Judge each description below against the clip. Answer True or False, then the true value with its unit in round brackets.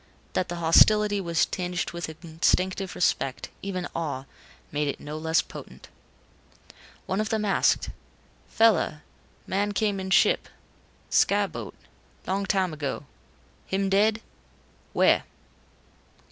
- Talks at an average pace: False (120 wpm)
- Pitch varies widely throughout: False (3.6 semitones)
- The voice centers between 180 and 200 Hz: True (185 Hz)